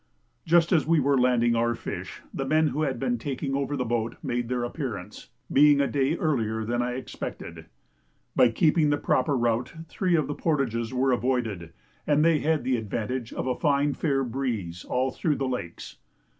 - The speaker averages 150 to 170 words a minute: No, average, 185 wpm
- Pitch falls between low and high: No, low, 130 Hz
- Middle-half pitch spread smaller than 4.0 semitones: Yes, average, 3.6 semitones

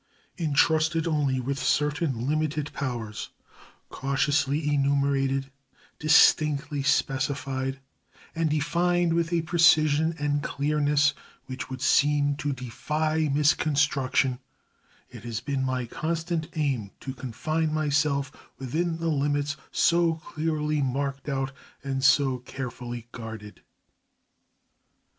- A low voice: No, medium, 145 Hz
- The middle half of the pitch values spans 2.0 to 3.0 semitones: Yes, narrow, 2.5 semitones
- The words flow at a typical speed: No, slow, 100 wpm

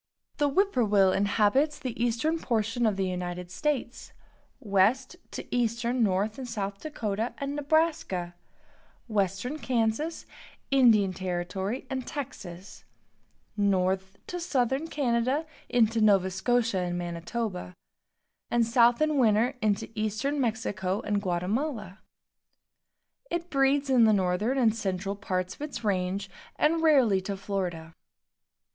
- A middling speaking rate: No, slow, 120 wpm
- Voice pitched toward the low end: No, high, 220 Hz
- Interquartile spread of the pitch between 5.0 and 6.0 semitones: Yes, average, 5.3 semitones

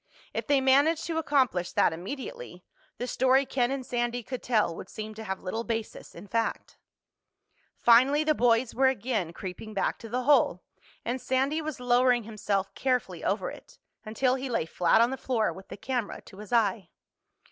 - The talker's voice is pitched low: No, high, 240 Hz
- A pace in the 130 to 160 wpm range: No, average, 180 wpm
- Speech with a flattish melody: No, average, 3.6 semitones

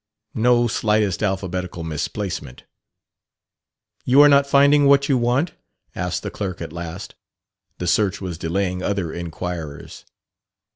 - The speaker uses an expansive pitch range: Yes, wide, 5.8 semitones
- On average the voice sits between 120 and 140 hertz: No, very low, 95 Hz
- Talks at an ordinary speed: No, slow, 125 wpm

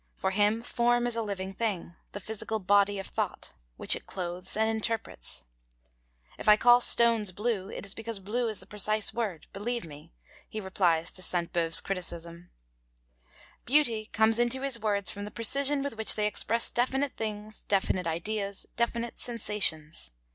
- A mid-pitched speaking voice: No, high, 210 Hz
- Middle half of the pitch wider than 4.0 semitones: No, average, 3.4 semitones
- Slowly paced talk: No, average, 165 wpm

